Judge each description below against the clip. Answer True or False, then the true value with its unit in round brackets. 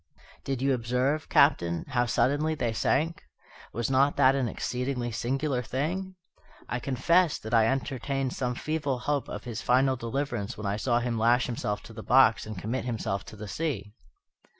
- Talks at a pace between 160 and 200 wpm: True (175 wpm)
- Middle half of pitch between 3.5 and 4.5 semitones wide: False (3.1 semitones)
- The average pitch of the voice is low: True (125 Hz)